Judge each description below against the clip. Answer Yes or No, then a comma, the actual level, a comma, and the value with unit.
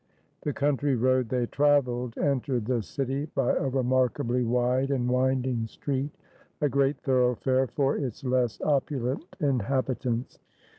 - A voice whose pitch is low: Yes, low, 130 Hz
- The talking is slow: Yes, slow, 130 wpm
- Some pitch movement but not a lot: No, narrow, 1.9 semitones